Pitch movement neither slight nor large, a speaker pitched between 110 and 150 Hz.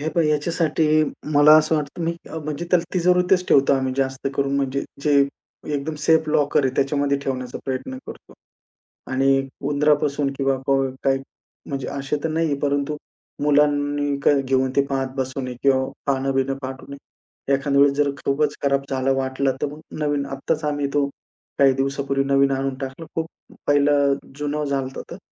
No: narrow, 1.6 semitones; medium, 140 Hz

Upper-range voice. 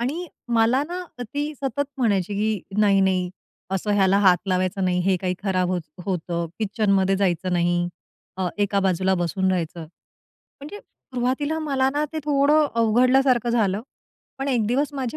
Yes: high, 205 Hz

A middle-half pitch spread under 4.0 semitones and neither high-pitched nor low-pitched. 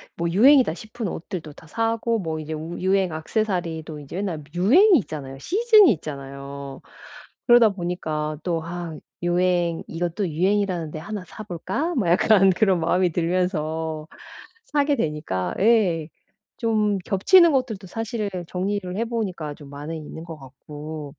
No: average, 5.2 semitones; medium, 175 Hz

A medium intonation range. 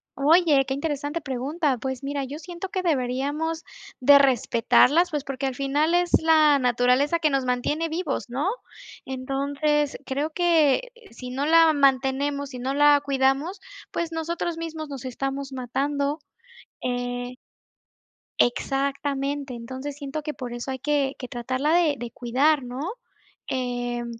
Yes: average, 3.1 semitones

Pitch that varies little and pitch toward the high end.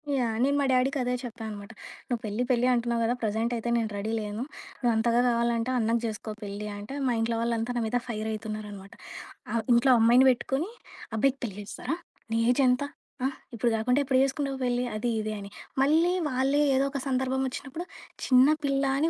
No: average, 3.1 semitones; high, 240 Hz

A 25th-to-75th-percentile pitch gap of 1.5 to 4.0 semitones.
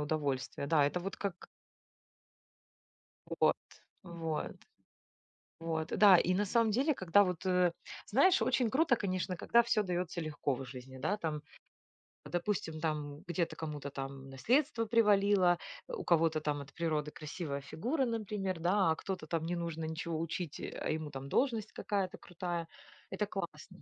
No: average, 4.6 semitones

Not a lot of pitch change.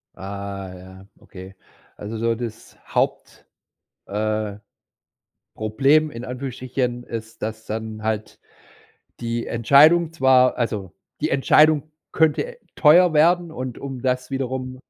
No: average, 4.2 semitones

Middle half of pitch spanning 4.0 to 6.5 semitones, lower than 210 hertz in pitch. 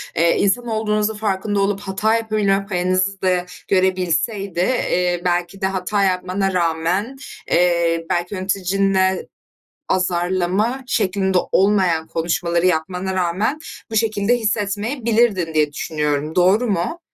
No: average, 2.7 semitones; high, 190 Hz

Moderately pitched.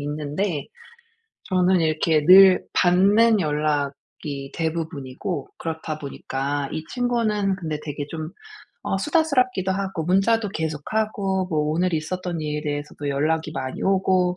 Yes: medium, 165 Hz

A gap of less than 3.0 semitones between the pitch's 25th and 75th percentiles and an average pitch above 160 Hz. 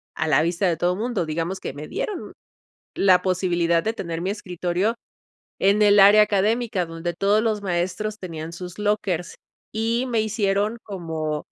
No: average, 3.7 semitones; high, 190 Hz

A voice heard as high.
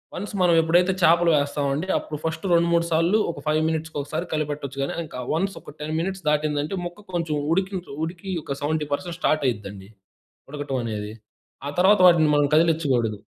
No: medium, 155 Hz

